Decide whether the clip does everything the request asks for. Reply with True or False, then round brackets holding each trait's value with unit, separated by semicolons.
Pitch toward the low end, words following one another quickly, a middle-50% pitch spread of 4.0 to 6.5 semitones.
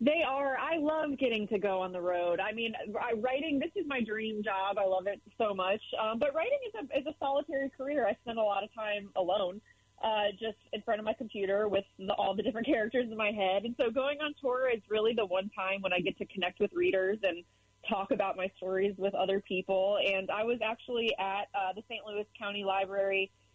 False (210 Hz; 230 wpm; 4.5 semitones)